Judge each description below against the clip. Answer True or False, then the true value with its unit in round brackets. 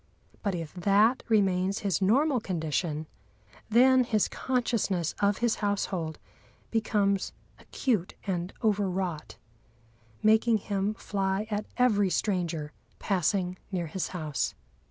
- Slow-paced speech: True (115 wpm)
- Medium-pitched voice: False (195 Hz)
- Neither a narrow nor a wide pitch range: True (3.3 semitones)